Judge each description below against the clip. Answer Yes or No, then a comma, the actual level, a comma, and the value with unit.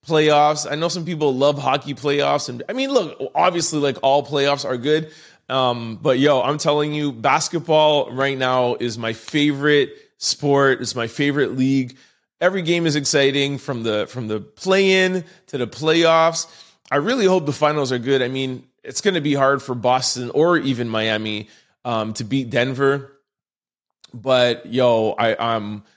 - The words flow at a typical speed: Yes, average, 170 wpm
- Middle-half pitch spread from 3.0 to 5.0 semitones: Yes, average, 3.6 semitones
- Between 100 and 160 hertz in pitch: Yes, medium, 140 Hz